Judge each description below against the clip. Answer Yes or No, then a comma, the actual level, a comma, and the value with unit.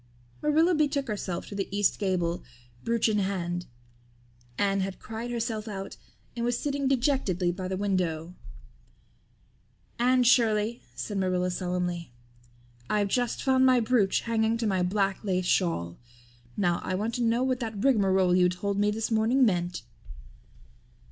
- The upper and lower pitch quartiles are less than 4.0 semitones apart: No, average, 4.3 semitones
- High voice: Yes, high, 205 Hz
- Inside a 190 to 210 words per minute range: No, average, 150 wpm